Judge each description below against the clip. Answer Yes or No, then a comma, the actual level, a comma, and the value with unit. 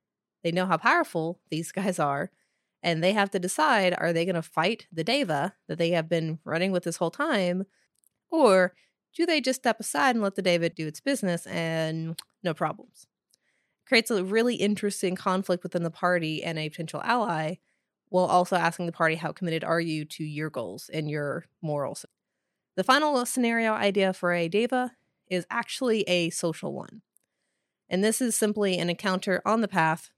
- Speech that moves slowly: No, average, 185 wpm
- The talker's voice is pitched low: No, medium, 180 Hz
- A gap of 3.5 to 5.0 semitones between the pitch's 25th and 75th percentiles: Yes, average, 3.9 semitones